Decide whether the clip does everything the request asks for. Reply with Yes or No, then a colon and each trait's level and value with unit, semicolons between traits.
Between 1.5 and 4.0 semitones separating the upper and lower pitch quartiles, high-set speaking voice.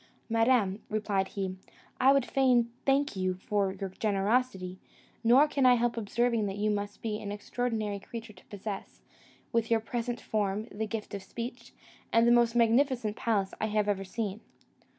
Yes: average, 2.9 semitones; high, 220 Hz